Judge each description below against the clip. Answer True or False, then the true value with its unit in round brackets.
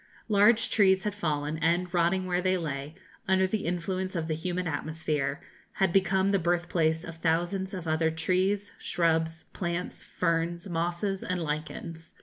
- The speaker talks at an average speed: True (150 wpm)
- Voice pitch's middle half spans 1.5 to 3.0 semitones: True (2.6 semitones)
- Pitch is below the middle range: False (175 Hz)